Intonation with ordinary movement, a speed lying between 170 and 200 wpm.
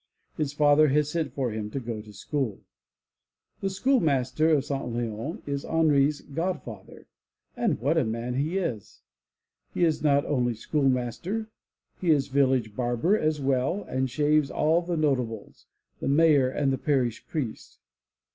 No: average, 4.0 semitones; average, 150 wpm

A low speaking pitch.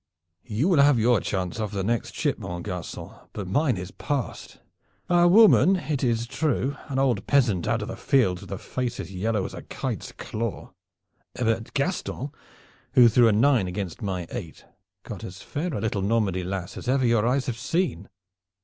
Yes: low, 115 Hz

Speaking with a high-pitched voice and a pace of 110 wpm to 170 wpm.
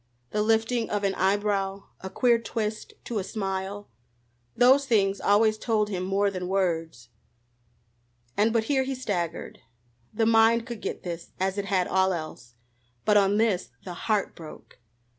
Yes: high, 205 Hz; average, 160 wpm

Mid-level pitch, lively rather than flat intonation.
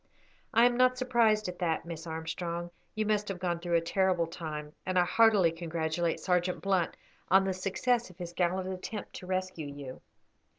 No: medium, 180 Hz; average, 2.7 semitones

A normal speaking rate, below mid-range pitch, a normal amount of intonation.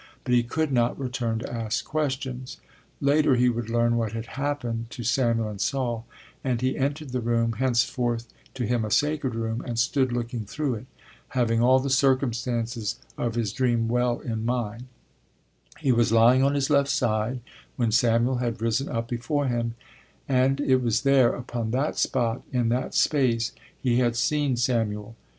No: average, 175 wpm; low, 120 Hz; narrow, 2.3 semitones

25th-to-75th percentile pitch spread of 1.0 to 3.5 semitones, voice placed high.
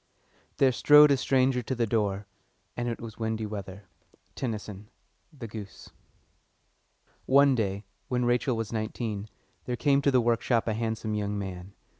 No: average, 3.2 semitones; low, 115 Hz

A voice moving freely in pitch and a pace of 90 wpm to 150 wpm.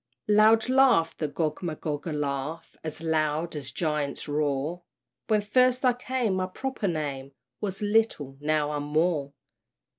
Yes: wide, 6.1 semitones; average, 140 wpm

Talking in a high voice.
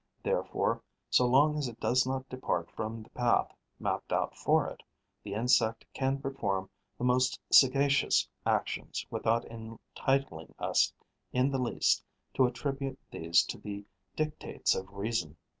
No: low, 125 Hz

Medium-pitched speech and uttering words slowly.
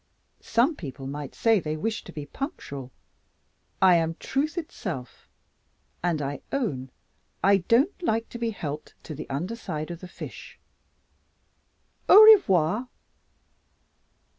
Yes: medium, 180 Hz; slow, 125 wpm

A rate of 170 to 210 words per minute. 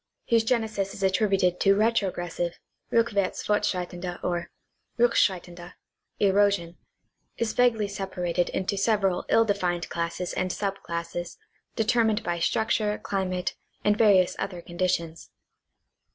No: slow, 135 wpm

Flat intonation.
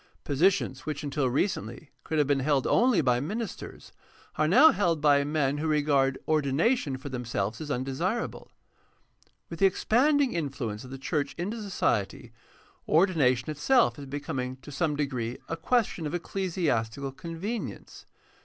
No: average, 5.1 semitones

